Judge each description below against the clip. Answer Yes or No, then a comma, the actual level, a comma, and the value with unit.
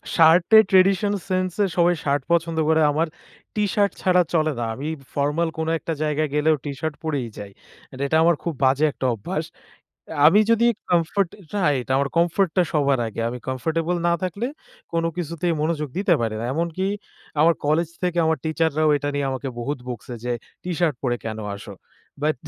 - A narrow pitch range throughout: No, average, 3.6 semitones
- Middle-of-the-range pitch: Yes, medium, 160 Hz